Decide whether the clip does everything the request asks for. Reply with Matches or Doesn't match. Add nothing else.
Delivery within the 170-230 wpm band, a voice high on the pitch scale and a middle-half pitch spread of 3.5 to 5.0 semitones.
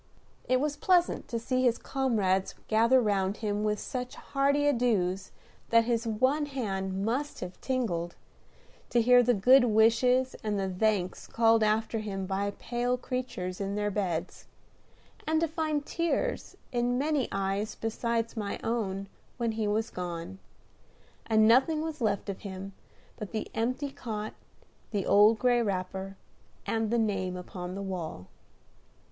Doesn't match